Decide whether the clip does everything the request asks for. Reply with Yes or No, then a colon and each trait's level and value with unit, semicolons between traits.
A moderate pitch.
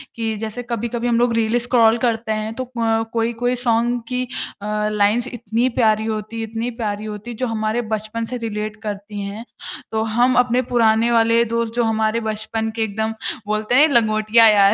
No: high, 225 Hz